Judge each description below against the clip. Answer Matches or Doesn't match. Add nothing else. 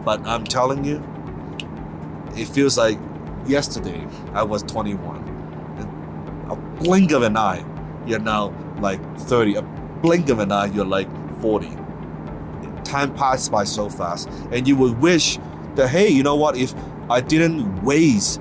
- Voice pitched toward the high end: Doesn't match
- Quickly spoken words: Doesn't match